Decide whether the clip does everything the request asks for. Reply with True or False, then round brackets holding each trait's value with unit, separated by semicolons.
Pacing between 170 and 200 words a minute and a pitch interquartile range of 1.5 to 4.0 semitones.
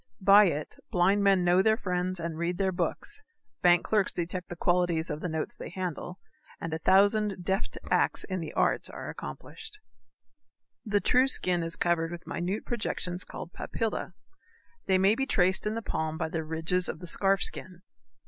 True (180 wpm; 2.6 semitones)